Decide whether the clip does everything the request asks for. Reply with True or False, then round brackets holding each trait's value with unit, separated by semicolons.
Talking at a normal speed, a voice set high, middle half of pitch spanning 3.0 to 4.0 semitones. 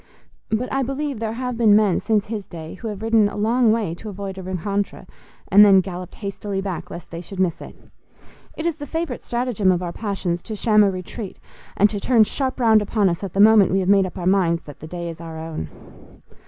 False (235 wpm; 200 Hz; 3.5 semitones)